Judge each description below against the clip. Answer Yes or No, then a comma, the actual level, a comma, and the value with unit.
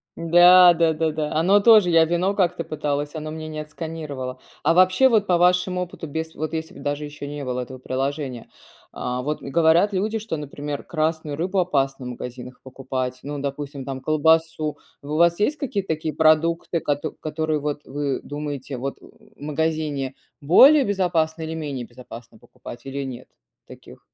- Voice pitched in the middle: Yes, medium, 155 Hz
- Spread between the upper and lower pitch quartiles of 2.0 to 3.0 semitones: No, average, 3.4 semitones